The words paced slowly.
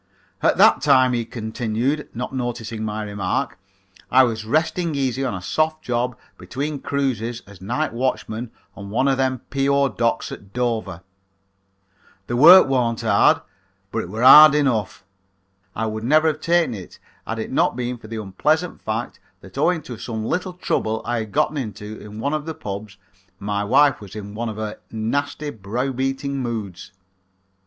No: average, 170 wpm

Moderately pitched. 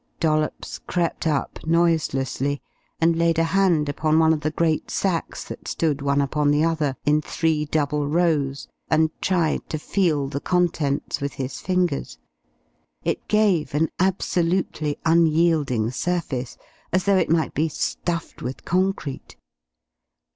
Yes: medium, 160 Hz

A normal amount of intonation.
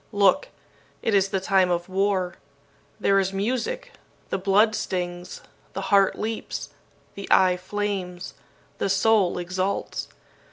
No: narrow, 1.8 semitones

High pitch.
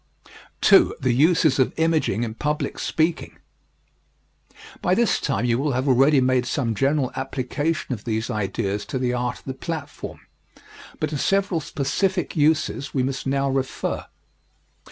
No: low, 135 Hz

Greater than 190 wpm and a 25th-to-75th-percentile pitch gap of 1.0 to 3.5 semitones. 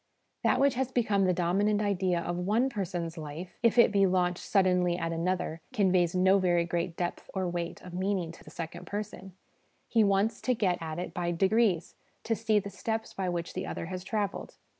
Yes: average, 200 wpm; average, 2.9 semitones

